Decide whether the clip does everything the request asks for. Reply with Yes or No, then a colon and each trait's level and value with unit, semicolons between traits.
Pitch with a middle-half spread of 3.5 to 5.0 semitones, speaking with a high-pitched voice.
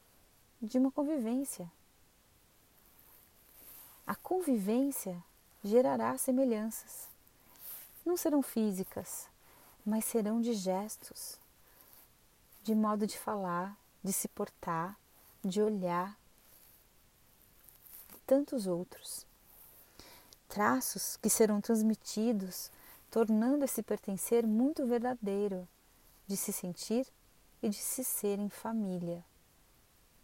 Yes: average, 3.8 semitones; high, 220 Hz